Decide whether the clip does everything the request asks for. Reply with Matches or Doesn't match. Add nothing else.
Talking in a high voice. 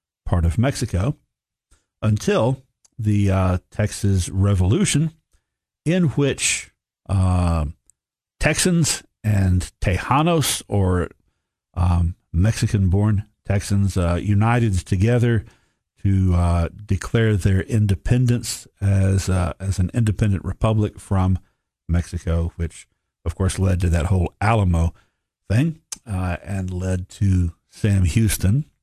Doesn't match